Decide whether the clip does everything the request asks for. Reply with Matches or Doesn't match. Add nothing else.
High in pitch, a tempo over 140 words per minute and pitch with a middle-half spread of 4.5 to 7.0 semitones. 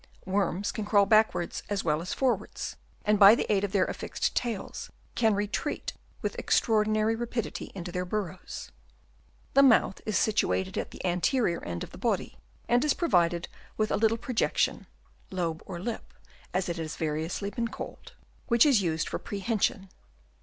Doesn't match